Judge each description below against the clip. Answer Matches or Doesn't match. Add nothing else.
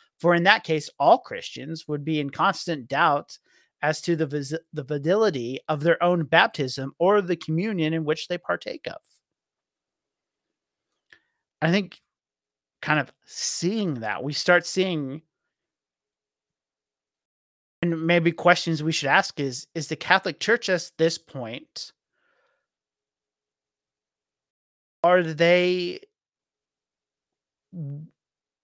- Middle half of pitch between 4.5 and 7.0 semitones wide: Matches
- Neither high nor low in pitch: Matches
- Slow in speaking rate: Matches